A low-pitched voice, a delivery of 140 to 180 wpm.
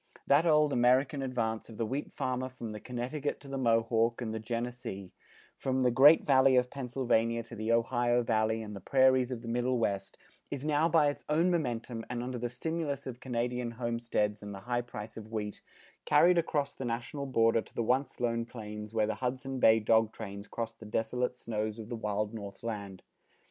No: low, 120 Hz; average, 200 wpm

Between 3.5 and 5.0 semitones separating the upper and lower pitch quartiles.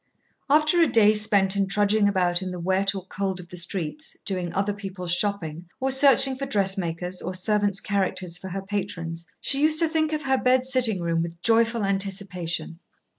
Yes: average, 4.2 semitones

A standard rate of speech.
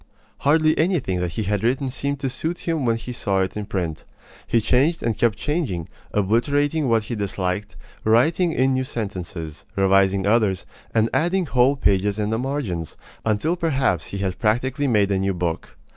Yes: average, 175 wpm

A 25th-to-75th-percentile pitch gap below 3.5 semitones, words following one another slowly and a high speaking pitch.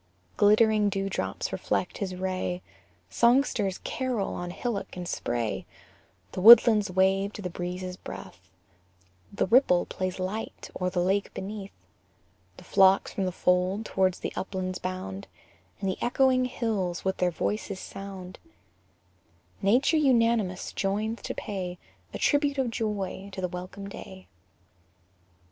Yes: average, 2.9 semitones; slow, 130 wpm; high, 195 Hz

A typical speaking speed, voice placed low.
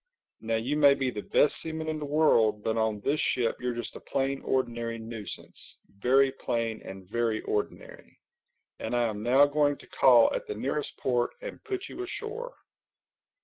Yes: average, 175 wpm; low, 125 Hz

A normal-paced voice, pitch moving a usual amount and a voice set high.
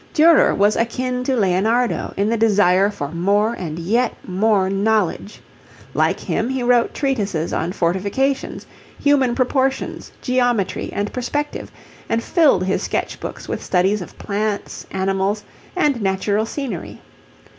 No: slow, 130 wpm; average, 4.5 semitones; high, 215 Hz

